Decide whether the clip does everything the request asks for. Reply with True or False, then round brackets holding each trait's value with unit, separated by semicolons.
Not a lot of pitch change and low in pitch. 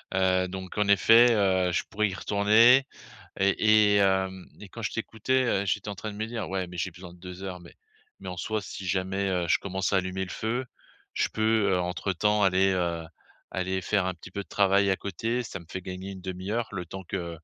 True (2.1 semitones; 95 Hz)